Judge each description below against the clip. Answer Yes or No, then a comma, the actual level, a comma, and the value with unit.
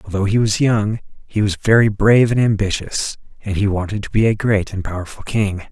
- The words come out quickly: Yes, fast, 220 wpm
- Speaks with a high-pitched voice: No, low, 105 Hz